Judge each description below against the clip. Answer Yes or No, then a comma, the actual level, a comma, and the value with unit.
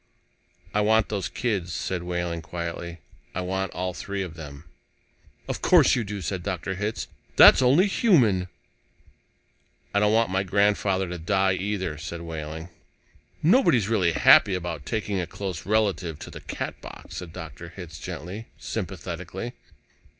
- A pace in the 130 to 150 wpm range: Yes, average, 145 wpm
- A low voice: Yes, very low, 95 Hz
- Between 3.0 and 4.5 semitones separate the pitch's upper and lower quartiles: Yes, average, 3.4 semitones